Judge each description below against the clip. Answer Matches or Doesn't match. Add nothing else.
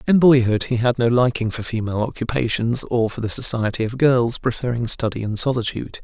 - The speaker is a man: Matches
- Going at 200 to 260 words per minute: Doesn't match